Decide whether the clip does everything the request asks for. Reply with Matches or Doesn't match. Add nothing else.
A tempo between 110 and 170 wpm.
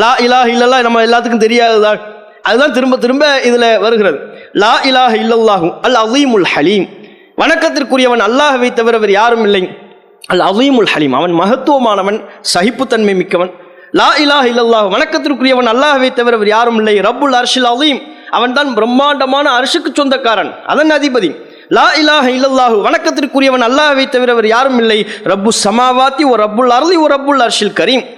Matches